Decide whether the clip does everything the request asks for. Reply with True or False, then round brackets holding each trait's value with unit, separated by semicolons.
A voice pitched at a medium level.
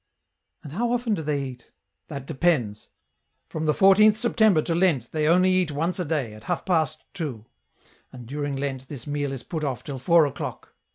True (155 Hz)